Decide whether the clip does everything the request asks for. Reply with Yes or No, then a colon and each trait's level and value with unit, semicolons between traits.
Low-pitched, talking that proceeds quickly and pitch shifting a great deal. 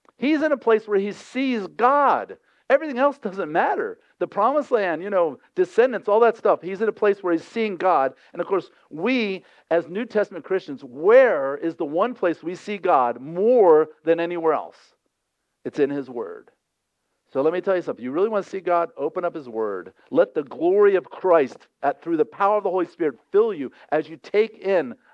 No: high, 210 Hz; fast, 210 wpm; wide, 8.9 semitones